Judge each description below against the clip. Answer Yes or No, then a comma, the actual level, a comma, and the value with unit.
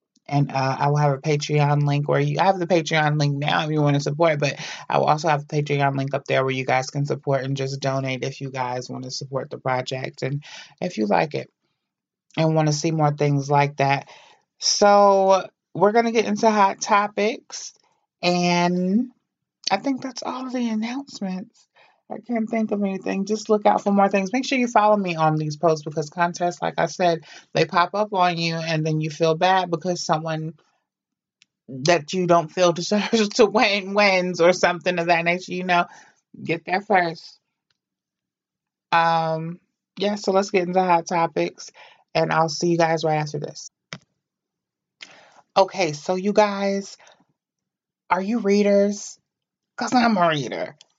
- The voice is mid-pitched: Yes, medium, 175 Hz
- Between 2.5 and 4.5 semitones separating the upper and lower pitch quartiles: No, average, 5.0 semitones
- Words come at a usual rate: Yes, average, 185 wpm